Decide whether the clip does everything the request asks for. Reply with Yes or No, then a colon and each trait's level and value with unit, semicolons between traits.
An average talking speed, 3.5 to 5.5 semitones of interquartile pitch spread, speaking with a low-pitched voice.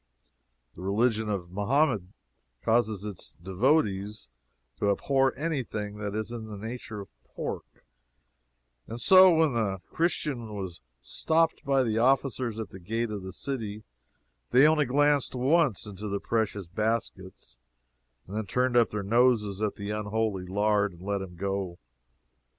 Yes: average, 145 wpm; average, 4.0 semitones; low, 110 Hz